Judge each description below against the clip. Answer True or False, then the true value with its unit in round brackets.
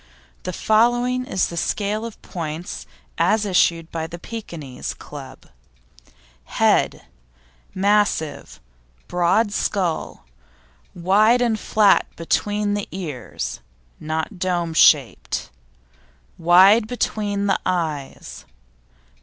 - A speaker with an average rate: False (95 wpm)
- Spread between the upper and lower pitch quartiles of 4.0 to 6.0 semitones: True (4.3 semitones)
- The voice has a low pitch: False (185 Hz)